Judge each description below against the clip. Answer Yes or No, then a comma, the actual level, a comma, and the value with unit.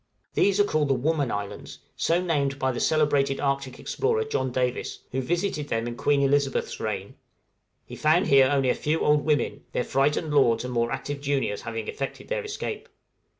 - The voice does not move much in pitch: No, average, 3.2 semitones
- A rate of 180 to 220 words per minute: Yes, average, 185 wpm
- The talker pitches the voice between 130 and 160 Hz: Yes, medium, 140 Hz